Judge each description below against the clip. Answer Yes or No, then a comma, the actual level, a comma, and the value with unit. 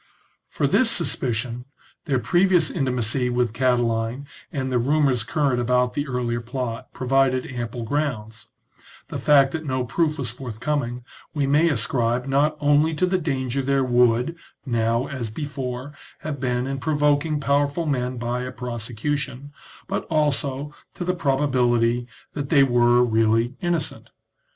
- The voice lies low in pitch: Yes, low, 130 Hz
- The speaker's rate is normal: Yes, average, 145 wpm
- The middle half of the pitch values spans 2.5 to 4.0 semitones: Yes, average, 3.1 semitones